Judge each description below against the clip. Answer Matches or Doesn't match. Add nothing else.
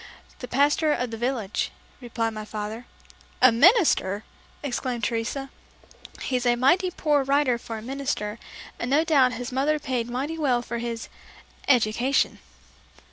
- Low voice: Doesn't match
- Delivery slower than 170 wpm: Matches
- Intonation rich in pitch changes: Doesn't match